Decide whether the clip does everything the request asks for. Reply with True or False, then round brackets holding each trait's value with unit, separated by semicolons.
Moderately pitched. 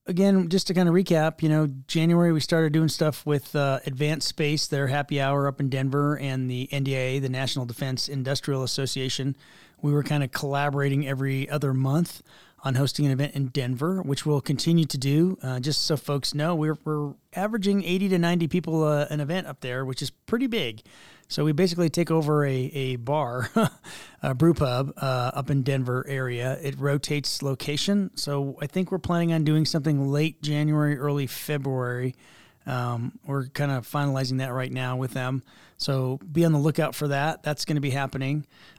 True (145 Hz)